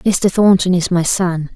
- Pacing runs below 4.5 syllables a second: Yes, 4.0 syllables/s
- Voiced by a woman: Yes, female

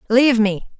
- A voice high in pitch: Yes, high, 230 Hz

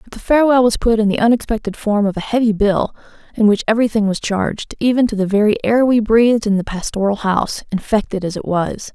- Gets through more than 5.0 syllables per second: Yes, 6.2 syllables/s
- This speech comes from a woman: Yes, female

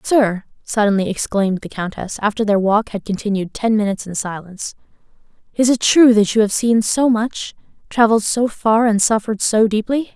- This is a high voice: Yes, high, 215 Hz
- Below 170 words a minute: No, average, 175 wpm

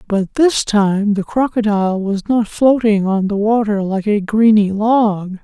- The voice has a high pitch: Yes, high, 210 Hz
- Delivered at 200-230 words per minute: No, average, 165 wpm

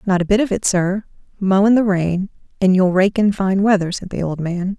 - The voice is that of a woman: Yes, female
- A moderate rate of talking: No, fast, 250 wpm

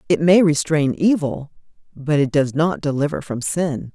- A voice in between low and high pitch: Yes, medium, 155 Hz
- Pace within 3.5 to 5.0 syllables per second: Yes, 4.5 syllables/s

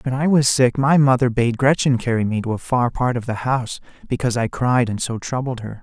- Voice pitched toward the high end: No, low, 125 Hz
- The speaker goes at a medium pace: No, fast, 245 wpm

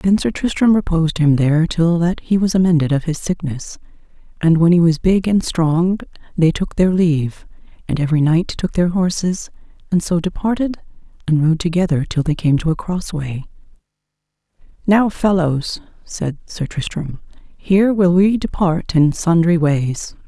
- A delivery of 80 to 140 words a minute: No, average, 165 wpm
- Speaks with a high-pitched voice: No, medium, 170 Hz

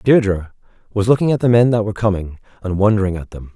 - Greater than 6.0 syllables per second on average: Yes, 6.6 syllables/s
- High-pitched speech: No, low, 105 Hz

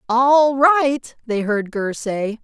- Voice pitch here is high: Yes, high, 245 Hz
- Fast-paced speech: No, average, 150 wpm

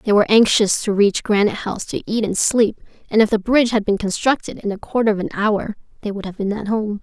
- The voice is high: Yes, high, 210 Hz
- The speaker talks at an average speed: No, fast, 255 wpm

